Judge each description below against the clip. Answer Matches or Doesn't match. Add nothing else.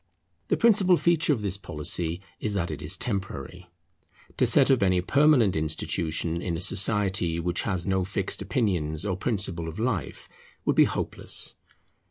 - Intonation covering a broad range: Doesn't match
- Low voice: Matches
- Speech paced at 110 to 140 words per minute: Doesn't match